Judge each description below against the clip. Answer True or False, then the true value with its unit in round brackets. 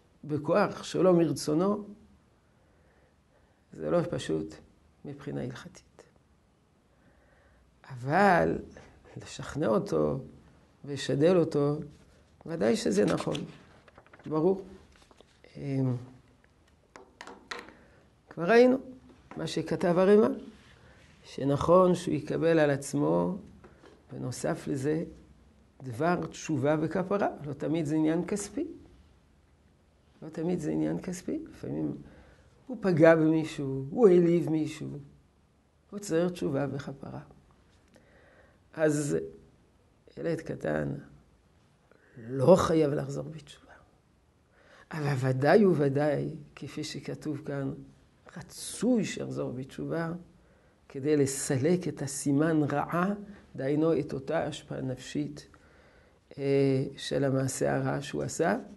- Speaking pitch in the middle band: True (145 Hz)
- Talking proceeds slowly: True (85 wpm)